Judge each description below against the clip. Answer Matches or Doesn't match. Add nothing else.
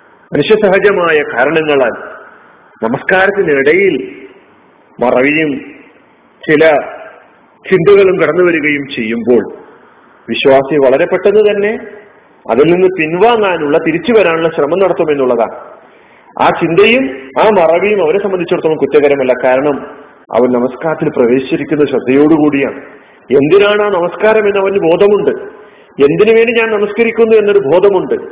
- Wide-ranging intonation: Matches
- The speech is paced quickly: Doesn't match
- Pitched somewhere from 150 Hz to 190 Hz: Matches